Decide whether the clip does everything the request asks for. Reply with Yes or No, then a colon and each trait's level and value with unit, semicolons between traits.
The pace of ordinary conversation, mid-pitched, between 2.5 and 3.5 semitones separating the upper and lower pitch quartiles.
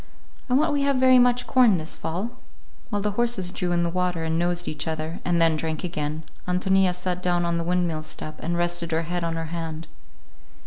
No: fast, 215 wpm; medium, 175 Hz; average, 2.8 semitones